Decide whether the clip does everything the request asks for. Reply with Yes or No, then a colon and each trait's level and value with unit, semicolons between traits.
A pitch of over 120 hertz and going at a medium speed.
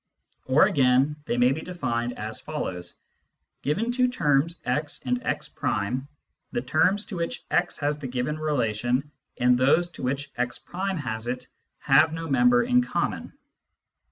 Yes: medium, 140 Hz; average, 155 wpm